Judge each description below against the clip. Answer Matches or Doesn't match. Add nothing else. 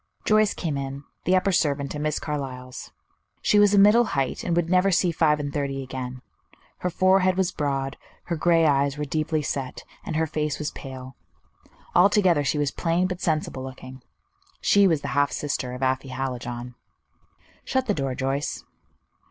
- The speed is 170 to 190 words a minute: Matches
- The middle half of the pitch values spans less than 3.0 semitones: Doesn't match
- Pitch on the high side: Doesn't match